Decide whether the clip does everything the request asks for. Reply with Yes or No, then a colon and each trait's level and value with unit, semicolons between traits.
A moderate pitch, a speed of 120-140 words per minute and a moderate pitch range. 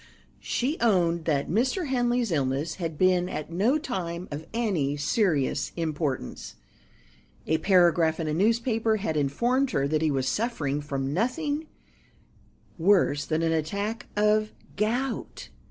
No: medium, 180 Hz; slow, 135 wpm; wide, 6.8 semitones